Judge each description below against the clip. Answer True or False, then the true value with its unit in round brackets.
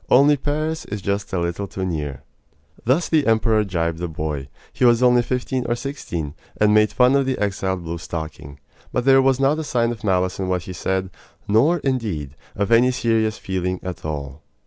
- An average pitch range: False (6.5 semitones)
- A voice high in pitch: False (105 Hz)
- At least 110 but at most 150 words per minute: False (195 wpm)